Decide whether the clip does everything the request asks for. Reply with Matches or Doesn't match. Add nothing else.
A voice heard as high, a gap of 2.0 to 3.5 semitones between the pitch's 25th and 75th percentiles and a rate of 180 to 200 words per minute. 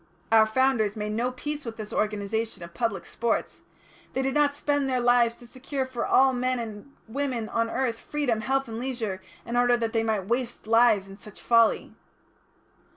Matches